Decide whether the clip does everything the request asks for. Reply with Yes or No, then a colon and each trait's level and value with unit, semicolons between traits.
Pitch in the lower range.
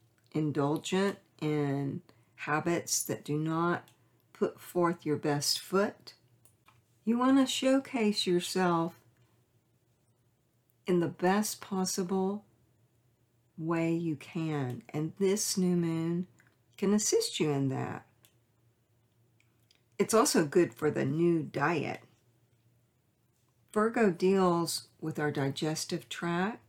No: medium, 150 Hz